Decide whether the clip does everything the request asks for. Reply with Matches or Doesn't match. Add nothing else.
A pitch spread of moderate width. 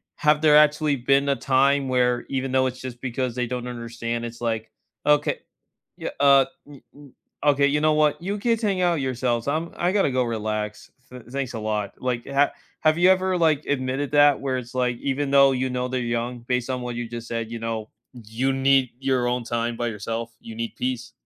Matches